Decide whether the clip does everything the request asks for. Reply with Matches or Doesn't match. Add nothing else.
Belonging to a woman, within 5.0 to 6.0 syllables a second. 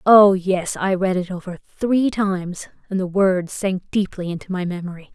Doesn't match